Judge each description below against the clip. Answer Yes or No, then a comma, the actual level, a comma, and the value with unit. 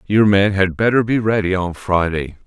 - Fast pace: No, average, 195 wpm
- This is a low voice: Yes, low, 100 Hz